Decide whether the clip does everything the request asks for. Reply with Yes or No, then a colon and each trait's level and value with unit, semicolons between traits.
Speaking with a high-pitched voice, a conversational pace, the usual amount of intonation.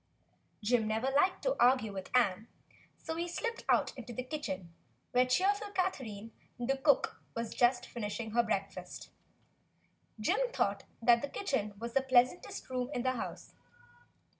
Yes: high, 245 Hz; average, 145 wpm; average, 3.6 semitones